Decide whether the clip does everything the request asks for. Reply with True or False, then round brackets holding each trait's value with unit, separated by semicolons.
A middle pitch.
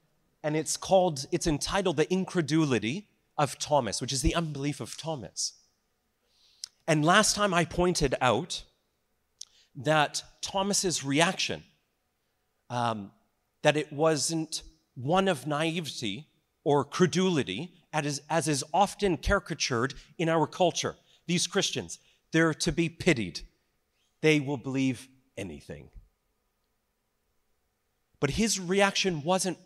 True (155 Hz)